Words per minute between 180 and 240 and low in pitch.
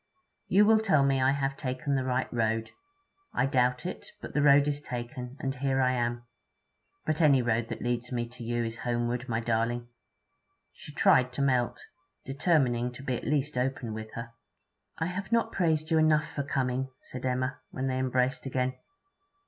Yes: average, 190 wpm; low, 130 Hz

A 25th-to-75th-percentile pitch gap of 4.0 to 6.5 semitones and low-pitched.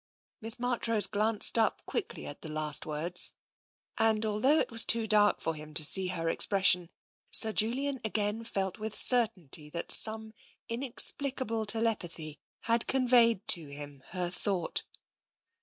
No: average, 5.0 semitones; high, 215 Hz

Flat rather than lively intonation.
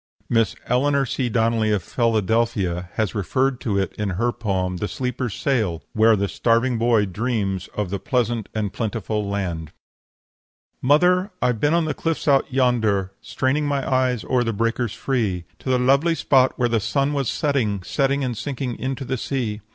No: average, 4.1 semitones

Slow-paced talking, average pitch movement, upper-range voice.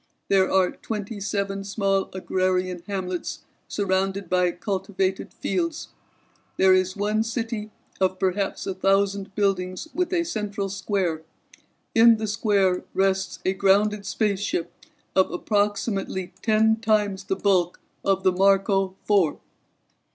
No: slow, 120 wpm; narrow, 1.7 semitones; high, 195 Hz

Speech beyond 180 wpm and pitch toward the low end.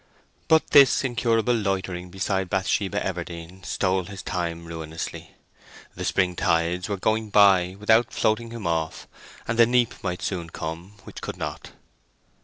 No: average, 145 wpm; very low, 95 Hz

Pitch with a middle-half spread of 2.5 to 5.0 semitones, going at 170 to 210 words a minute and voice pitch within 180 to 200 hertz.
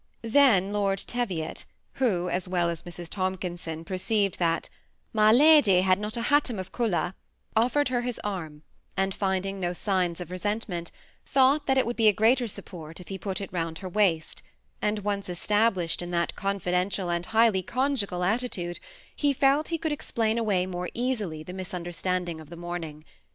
Yes: average, 4.4 semitones; average, 175 wpm; high, 190 Hz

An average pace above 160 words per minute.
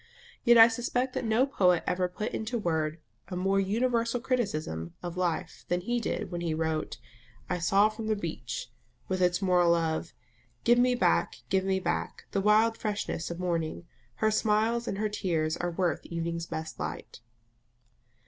Yes: average, 170 wpm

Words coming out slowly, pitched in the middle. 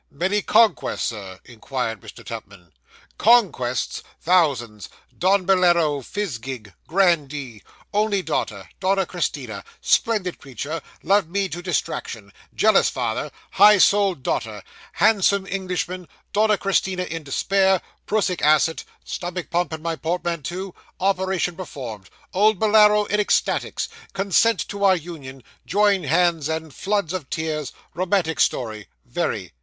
Yes: slow, 120 wpm; medium, 175 Hz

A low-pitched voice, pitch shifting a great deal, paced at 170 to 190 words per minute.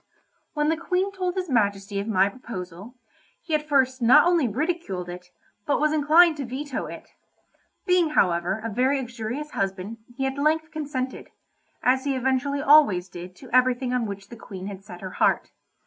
No: very high, 255 Hz; wide, 7.1 semitones; average, 175 wpm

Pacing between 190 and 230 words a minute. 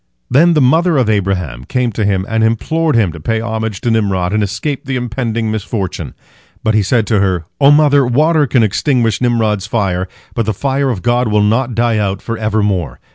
Yes: average, 200 wpm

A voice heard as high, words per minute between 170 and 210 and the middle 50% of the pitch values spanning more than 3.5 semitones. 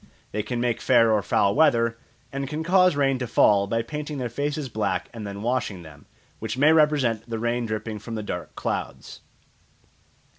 No: low, 120 Hz; average, 185 wpm; average, 4.7 semitones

